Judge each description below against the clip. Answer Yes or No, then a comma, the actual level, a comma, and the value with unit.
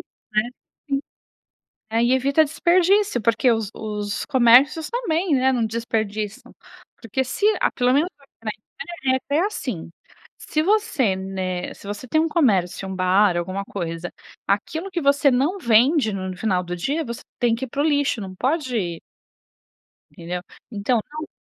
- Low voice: No, high, 240 Hz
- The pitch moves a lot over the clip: Yes, wide, 6.4 semitones